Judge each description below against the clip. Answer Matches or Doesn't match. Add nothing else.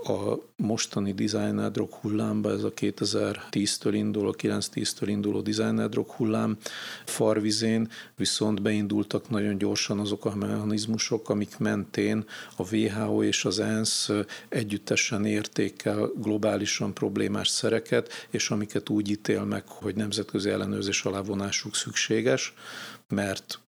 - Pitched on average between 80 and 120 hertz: Matches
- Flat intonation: Matches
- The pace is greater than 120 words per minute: Doesn't match